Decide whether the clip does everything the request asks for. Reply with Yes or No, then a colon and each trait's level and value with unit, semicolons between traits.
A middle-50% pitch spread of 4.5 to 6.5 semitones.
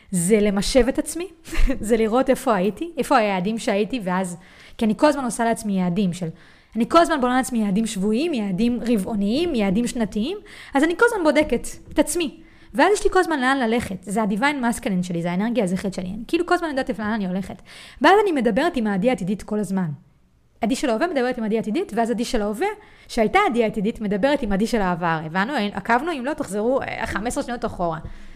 Yes: average, 5.0 semitones